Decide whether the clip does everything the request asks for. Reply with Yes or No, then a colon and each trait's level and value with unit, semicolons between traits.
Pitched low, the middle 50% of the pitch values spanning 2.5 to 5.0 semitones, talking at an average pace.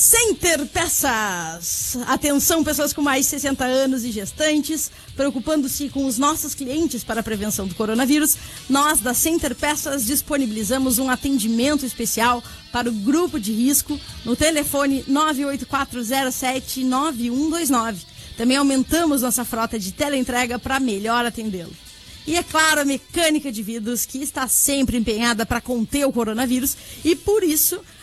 No: very high, 270 Hz; average, 3.5 semitones; average, 135 wpm